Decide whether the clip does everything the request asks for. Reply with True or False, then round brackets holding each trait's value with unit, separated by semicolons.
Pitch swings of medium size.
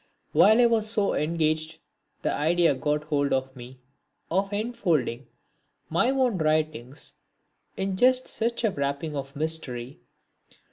False (6.4 semitones)